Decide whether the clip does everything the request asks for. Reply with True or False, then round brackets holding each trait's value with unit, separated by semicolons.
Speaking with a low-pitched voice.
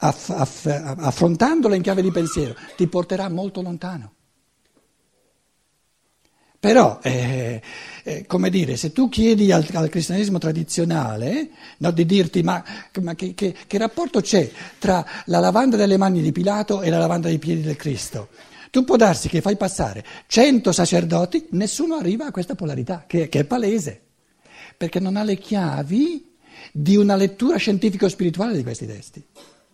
False (180 Hz)